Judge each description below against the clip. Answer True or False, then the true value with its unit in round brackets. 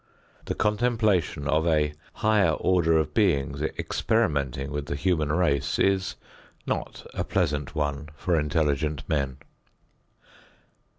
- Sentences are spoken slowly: True (115 wpm)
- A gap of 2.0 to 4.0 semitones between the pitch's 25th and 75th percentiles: False (4.4 semitones)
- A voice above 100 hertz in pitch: False (75 Hz)